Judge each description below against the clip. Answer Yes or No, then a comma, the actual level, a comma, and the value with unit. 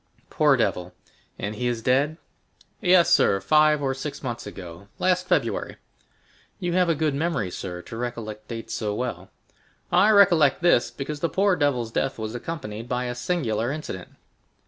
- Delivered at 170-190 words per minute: No, average, 160 wpm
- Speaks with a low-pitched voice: Yes, low, 130 Hz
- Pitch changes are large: Yes, wide, 6.4 semitones